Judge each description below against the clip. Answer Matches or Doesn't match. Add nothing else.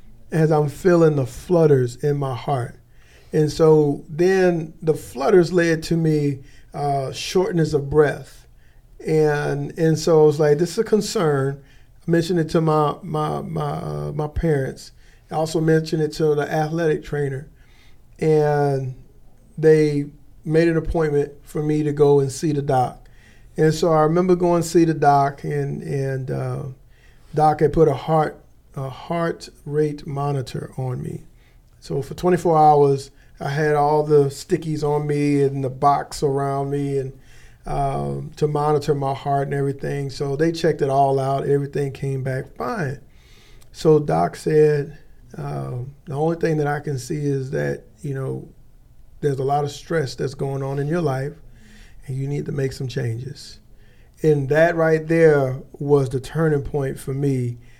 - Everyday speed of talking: Matches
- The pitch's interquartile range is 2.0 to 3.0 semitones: Matches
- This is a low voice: Doesn't match